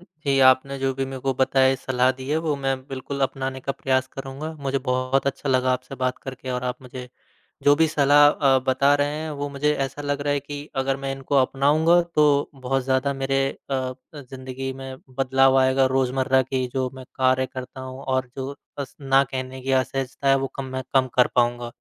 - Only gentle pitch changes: Yes, narrow, 1.1 semitones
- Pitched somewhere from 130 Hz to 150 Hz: Yes, low, 135 Hz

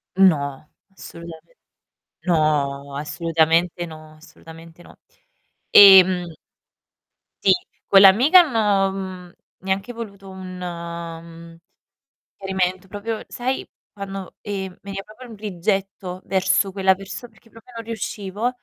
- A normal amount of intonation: Yes, average, 3.0 semitones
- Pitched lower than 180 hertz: No, high, 190 Hz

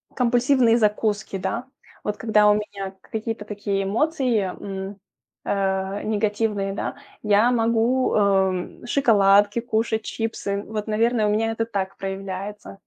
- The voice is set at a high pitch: Yes, high, 210 Hz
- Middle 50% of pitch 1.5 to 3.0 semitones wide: Yes, narrow, 2.4 semitones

